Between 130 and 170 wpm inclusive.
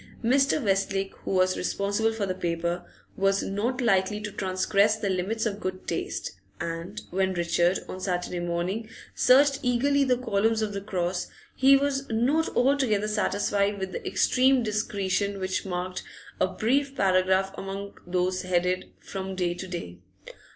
Yes: average, 150 wpm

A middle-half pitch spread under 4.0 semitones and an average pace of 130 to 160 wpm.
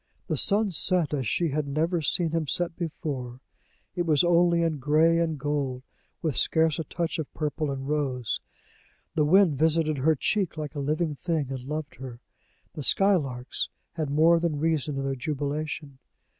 No: average, 3.0 semitones; average, 170 wpm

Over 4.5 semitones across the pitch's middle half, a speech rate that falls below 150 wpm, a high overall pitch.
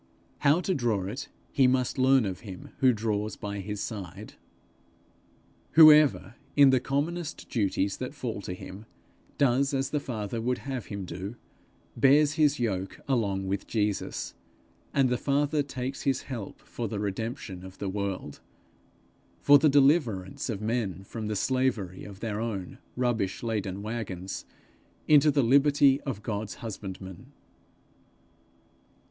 No: wide, 5.4 semitones; average, 140 wpm; low, 115 Hz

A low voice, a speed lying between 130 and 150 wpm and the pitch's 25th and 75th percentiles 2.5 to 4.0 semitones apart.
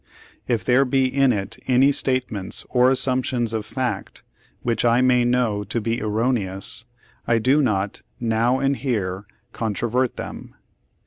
Yes: low, 120 Hz; average, 140 wpm; average, 3.0 semitones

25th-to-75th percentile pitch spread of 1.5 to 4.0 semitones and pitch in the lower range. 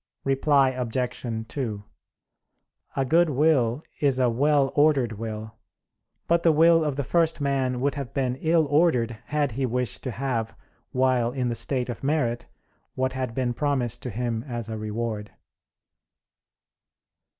Yes: average, 3.5 semitones; low, 130 Hz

